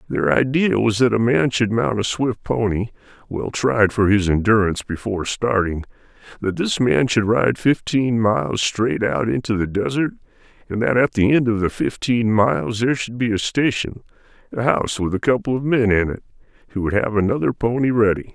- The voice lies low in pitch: Yes, low, 110 Hz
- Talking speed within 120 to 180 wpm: No, average, 195 wpm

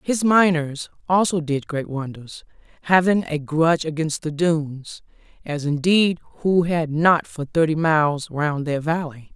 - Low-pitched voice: No, medium, 160 Hz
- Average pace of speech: Yes, average, 145 wpm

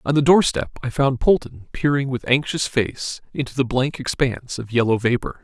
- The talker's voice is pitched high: No, low, 130 Hz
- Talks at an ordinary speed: Yes, average, 190 wpm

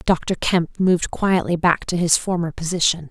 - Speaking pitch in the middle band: Yes, medium, 175 Hz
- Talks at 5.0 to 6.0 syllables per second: No, 4.7 syllables/s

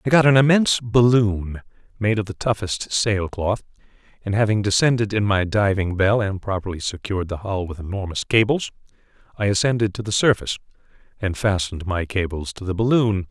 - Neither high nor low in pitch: No, low, 105 Hz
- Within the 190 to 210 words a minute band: No, average, 170 wpm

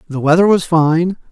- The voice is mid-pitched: Yes, medium, 165 Hz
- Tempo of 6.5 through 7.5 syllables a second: No, 4.7 syllables/s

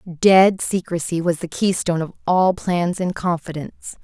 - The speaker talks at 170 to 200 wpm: No, average, 150 wpm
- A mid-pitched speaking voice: Yes, medium, 175 Hz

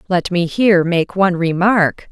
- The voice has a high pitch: No, medium, 180 Hz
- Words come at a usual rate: Yes, average, 170 wpm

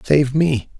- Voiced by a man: Yes, male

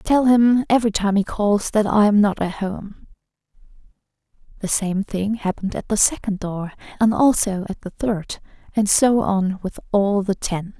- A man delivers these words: No, female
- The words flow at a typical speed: Yes, average, 180 wpm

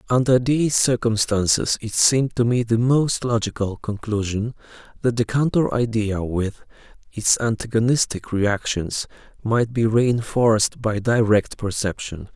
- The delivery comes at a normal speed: No, slow, 120 wpm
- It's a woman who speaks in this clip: No, male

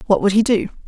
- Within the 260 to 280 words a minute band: Yes, fast, 275 wpm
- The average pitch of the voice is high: Yes, high, 205 Hz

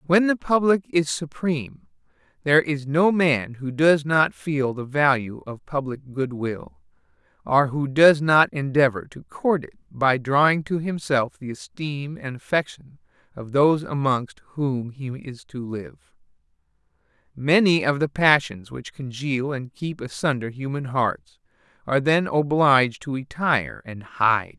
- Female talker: No, male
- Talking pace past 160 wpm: No, average, 155 wpm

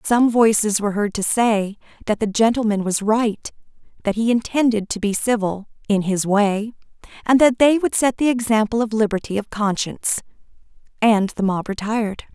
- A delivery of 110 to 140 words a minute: No, average, 165 wpm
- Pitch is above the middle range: Yes, high, 220 Hz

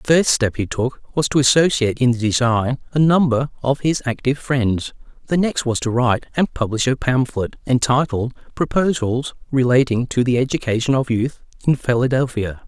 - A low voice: Yes, low, 130 Hz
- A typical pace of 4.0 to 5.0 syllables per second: No, 5.2 syllables/s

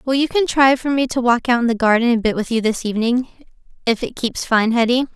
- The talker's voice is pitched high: Yes, high, 240 Hz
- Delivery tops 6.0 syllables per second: Yes, 6.3 syllables/s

